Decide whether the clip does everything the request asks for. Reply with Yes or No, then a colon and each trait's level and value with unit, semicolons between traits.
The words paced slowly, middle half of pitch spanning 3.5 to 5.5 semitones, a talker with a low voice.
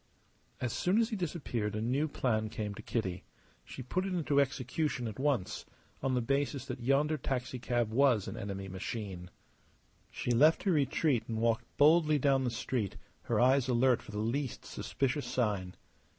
No: average, 170 wpm; average, 4.3 semitones; low, 125 Hz